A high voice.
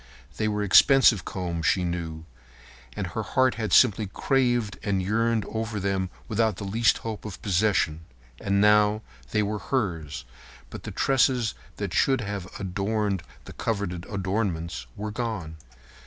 No: low, 105 Hz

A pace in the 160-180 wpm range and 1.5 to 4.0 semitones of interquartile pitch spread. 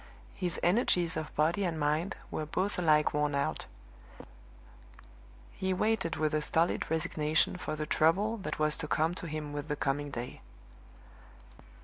No: average, 150 wpm; average, 2.9 semitones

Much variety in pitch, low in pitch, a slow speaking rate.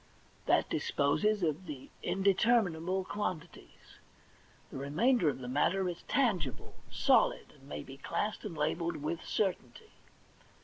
No: wide, 5.8 semitones; medium, 175 Hz; slow, 125 wpm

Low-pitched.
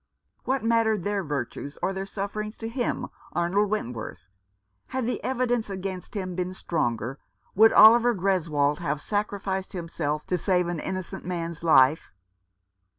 No: high, 190 Hz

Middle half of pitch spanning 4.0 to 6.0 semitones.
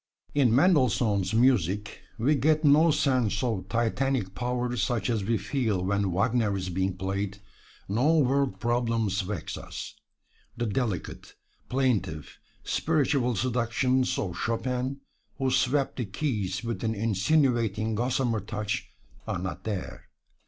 Yes: average, 4.5 semitones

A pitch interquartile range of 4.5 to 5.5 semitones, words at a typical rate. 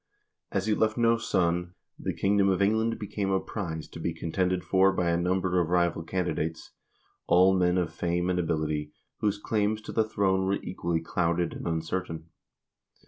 No: narrow, 2.6 semitones; average, 175 wpm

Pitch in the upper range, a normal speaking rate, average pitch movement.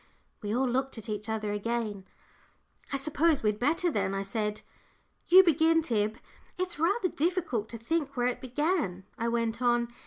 No: high, 240 Hz; average, 165 wpm; wide, 6.7 semitones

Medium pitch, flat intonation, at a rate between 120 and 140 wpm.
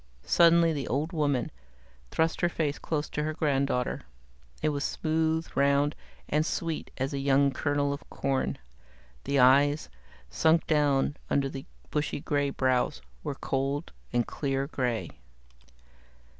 Yes: medium, 145 Hz; narrow, 2.2 semitones; slow, 135 wpm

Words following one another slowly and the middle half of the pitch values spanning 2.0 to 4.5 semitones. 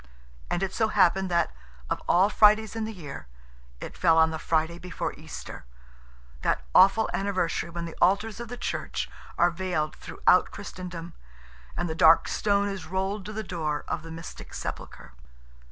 No: average, 170 wpm; average, 3.5 semitones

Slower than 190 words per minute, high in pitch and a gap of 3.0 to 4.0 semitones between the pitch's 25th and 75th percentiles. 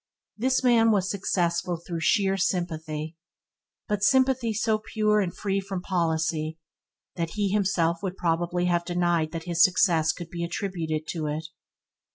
No: average, 150 wpm; medium, 175 Hz; average, 3.4 semitones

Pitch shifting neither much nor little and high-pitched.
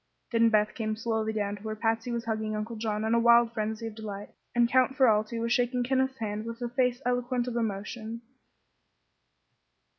No: narrow, 1.9 semitones; high, 230 Hz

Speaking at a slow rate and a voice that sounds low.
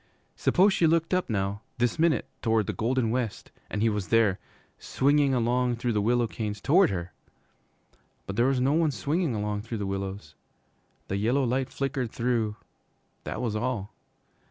No: average, 170 wpm; low, 120 Hz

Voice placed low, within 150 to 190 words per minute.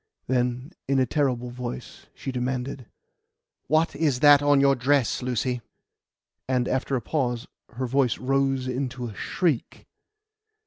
No: low, 130 Hz; slow, 135 wpm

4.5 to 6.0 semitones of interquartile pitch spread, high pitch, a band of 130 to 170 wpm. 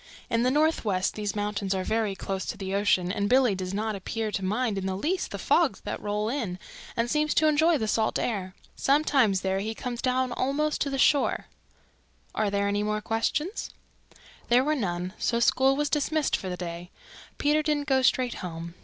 No: wide, 5.6 semitones; high, 220 Hz; average, 200 wpm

